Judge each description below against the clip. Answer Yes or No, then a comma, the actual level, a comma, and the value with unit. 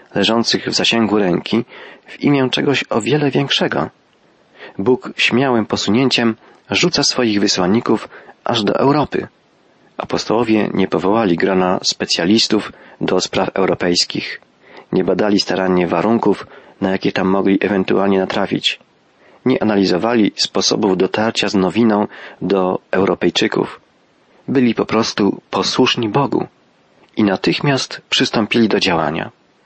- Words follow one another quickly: No, slow, 110 wpm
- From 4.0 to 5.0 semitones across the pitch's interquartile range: No, average, 3.3 semitones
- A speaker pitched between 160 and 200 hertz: No, low, 105 Hz